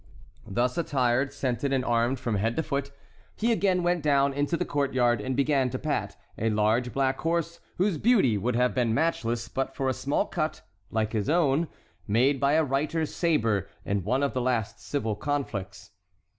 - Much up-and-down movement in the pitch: No, average, 3.8 semitones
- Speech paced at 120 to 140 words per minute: No, average, 185 wpm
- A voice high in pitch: No, low, 135 Hz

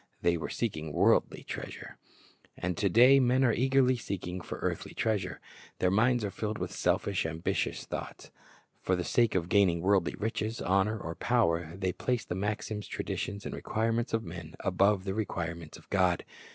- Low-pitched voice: Yes, low, 100 Hz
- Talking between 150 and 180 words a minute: Yes, average, 170 wpm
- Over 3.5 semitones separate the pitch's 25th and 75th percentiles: Yes, average, 4.1 semitones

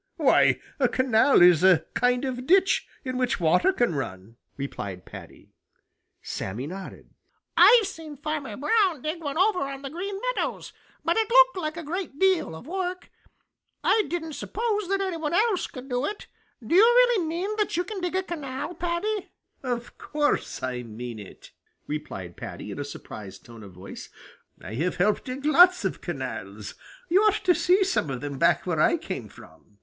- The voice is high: Yes, very high, 305 Hz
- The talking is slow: No, average, 180 wpm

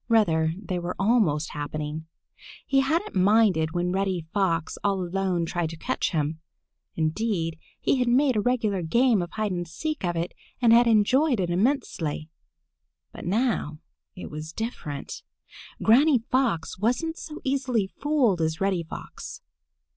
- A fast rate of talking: No, average, 145 wpm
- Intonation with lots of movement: Yes, wide, 6.5 semitones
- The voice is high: Yes, high, 195 Hz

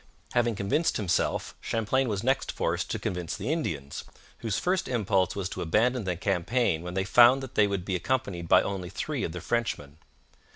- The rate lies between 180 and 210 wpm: Yes, average, 190 wpm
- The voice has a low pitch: Yes, low, 100 Hz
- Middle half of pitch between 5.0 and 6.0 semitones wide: Yes, wide, 5.5 semitones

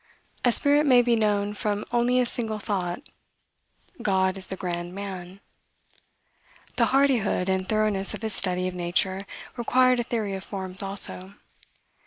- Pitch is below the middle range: No, high, 200 Hz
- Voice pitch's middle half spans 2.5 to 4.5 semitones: Yes, average, 3.8 semitones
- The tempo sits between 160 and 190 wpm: No, average, 150 wpm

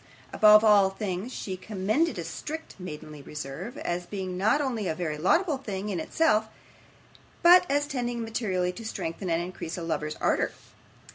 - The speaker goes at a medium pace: Yes, average, 160 wpm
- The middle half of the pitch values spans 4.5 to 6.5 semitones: Yes, average, 5.3 semitones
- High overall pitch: Yes, high, 195 Hz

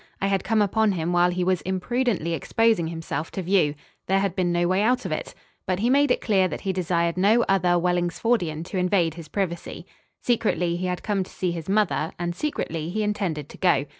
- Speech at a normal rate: No, fast, 215 wpm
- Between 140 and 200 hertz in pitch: Yes, medium, 185 Hz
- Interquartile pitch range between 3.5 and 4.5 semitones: No, average, 3.1 semitones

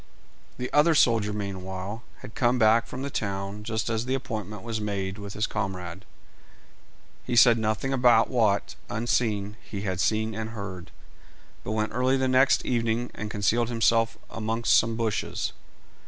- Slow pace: No, average, 155 wpm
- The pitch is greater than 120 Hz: No, low, 110 Hz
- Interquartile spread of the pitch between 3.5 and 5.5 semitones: No, narrow, 2.6 semitones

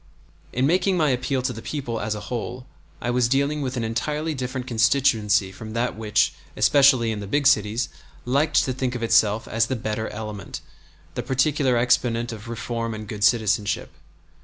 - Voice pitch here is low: Yes, low, 120 Hz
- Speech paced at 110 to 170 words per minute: No, average, 180 wpm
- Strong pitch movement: No, average, 3.2 semitones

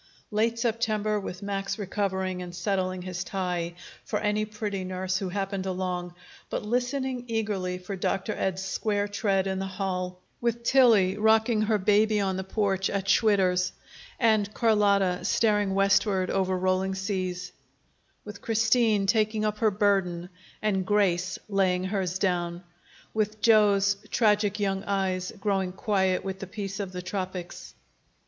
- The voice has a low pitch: No, high, 195 Hz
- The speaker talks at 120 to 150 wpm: Yes, average, 145 wpm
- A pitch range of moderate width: No, narrow, 2.2 semitones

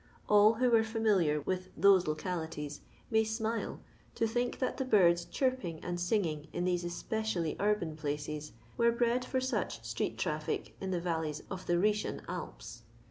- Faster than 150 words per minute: Yes, average, 165 wpm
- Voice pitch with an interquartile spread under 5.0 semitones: No, wide, 5.4 semitones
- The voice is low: No, medium, 185 Hz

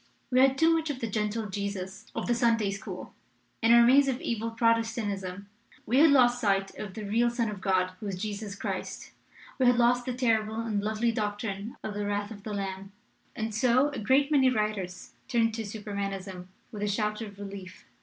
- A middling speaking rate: No, fast, 210 wpm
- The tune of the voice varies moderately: Yes, average, 3.0 semitones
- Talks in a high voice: Yes, high, 215 Hz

